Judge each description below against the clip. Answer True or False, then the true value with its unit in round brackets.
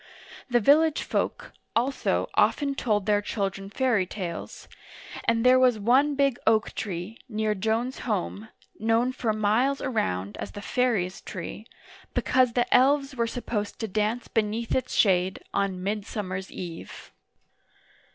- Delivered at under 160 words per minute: True (140 wpm)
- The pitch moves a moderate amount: True (4.0 semitones)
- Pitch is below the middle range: False (220 Hz)